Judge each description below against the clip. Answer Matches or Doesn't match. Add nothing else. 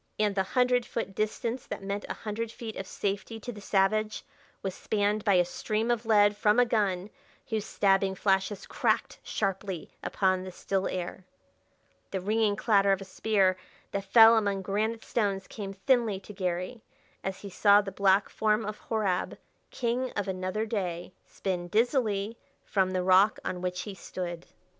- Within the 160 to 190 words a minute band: Matches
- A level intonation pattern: Matches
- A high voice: Matches